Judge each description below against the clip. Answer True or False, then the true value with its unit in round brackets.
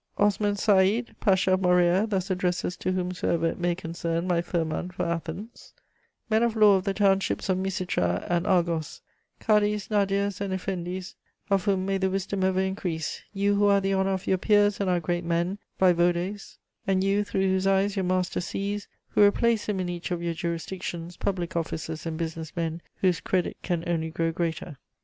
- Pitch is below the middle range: False (185 Hz)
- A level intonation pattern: True (2.3 semitones)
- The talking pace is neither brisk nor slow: True (185 wpm)